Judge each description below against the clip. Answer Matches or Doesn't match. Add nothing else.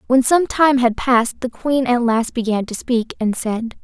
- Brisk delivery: Matches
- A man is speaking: Doesn't match